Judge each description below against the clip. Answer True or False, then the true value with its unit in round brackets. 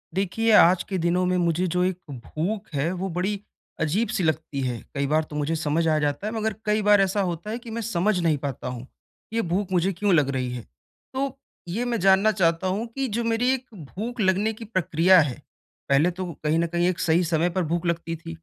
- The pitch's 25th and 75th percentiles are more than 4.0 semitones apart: True (4.5 semitones)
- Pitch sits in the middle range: True (180 Hz)